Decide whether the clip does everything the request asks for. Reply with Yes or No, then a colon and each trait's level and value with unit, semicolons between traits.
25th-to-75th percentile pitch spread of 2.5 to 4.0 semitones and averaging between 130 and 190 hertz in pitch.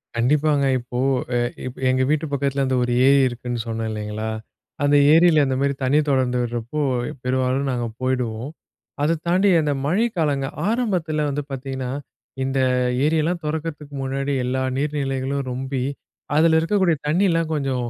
Yes: average, 3.2 semitones; medium, 140 Hz